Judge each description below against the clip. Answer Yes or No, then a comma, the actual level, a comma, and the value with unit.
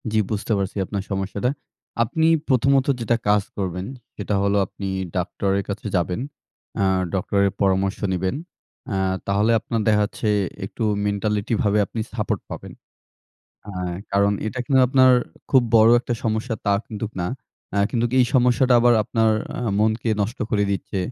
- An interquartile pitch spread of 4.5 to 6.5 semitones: No, average, 2.9 semitones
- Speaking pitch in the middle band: No, low, 105 Hz